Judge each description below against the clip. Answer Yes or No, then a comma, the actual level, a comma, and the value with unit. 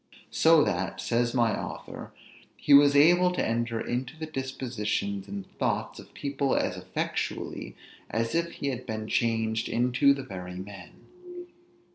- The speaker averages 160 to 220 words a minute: No, average, 145 wpm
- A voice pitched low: Yes, low, 120 Hz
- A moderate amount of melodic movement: Yes, average, 4.9 semitones